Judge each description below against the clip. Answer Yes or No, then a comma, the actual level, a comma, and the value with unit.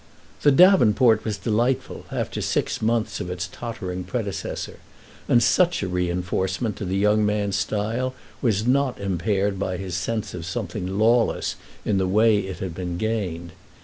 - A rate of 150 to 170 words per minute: Yes, average, 160 wpm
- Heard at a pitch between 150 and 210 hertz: No, low, 105 Hz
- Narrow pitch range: No, average, 3.8 semitones